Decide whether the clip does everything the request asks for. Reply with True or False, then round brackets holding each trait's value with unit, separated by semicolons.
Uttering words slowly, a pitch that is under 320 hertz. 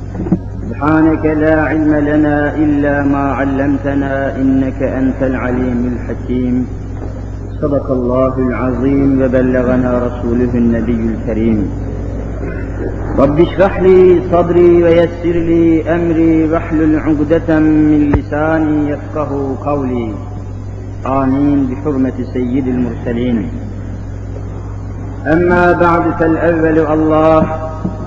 True (85 wpm; 135 Hz)